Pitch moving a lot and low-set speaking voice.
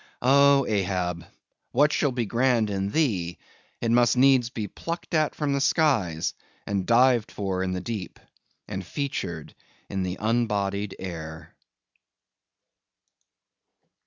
Yes: wide, 5.9 semitones; low, 110 Hz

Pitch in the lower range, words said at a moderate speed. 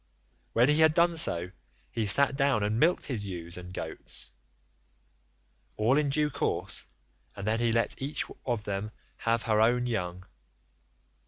Yes: low, 115 Hz; average, 150 wpm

